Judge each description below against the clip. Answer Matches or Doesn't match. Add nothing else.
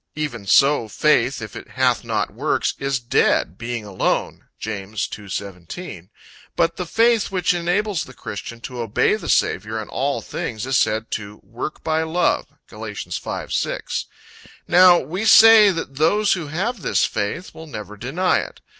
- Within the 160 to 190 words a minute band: Matches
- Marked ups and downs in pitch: Matches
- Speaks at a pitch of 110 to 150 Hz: Matches